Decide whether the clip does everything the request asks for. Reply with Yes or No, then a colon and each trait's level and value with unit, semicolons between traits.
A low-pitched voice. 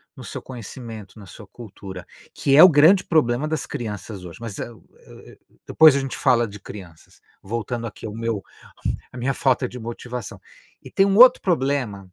Yes: low, 120 Hz